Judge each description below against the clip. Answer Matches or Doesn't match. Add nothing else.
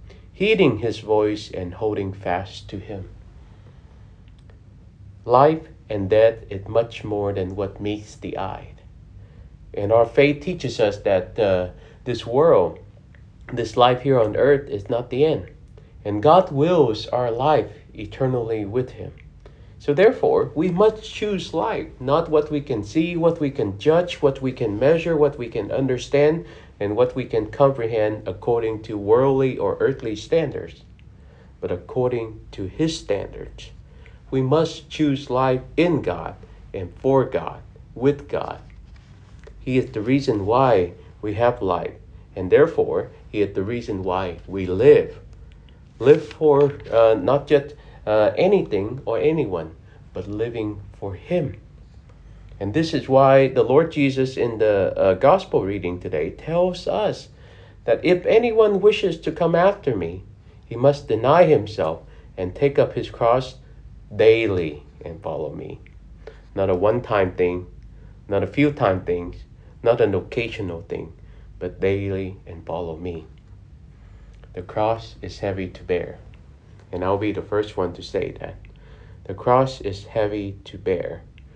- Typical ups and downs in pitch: Doesn't match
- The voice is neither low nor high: Doesn't match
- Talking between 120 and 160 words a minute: Matches